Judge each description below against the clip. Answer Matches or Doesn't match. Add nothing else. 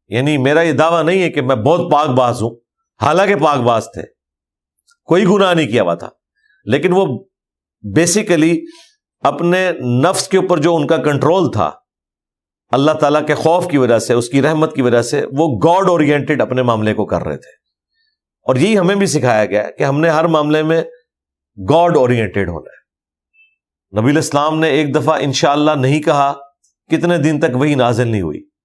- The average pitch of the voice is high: Doesn't match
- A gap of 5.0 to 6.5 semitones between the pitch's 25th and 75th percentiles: Matches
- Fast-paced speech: Doesn't match